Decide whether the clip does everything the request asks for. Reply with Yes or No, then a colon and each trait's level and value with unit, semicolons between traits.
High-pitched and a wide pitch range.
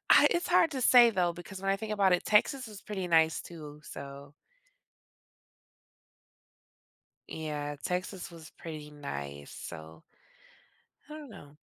No: medium, 170 Hz; wide, 6.1 semitones